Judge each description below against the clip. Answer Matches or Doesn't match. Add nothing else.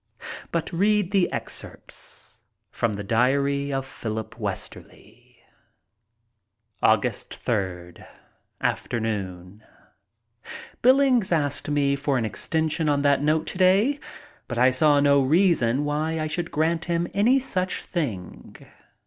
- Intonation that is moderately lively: Doesn't match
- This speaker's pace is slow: Matches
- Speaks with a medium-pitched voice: Matches